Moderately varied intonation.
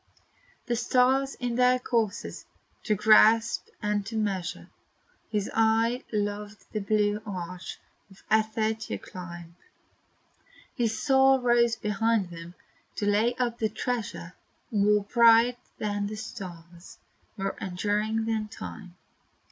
No: narrow, 2.3 semitones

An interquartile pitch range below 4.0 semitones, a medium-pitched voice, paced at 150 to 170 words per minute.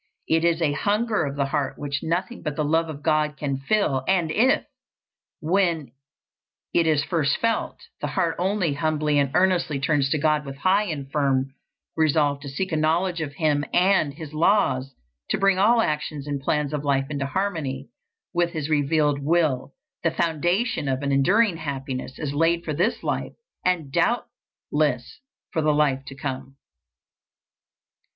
Yes: average, 3.4 semitones; medium, 155 Hz; average, 165 wpm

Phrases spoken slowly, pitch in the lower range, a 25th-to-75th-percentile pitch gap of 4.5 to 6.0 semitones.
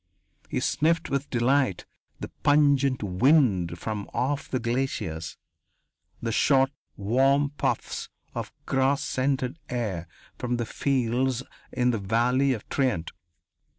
No: slow, 120 wpm; low, 130 Hz; average, 3.3 semitones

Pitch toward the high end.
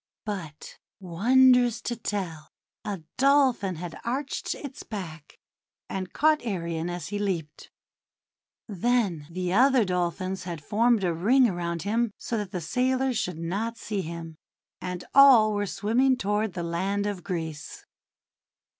Yes: high, 200 Hz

